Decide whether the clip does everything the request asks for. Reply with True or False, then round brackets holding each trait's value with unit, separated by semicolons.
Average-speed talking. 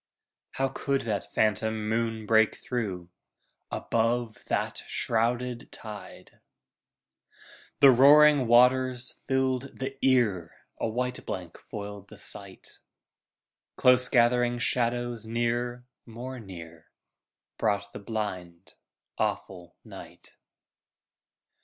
False (95 wpm)